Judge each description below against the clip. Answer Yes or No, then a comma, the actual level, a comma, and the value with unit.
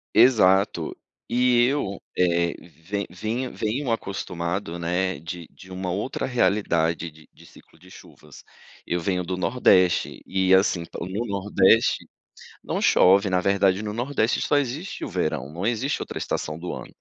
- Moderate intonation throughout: Yes, average, 4.2 semitones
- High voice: No, very low, 95 Hz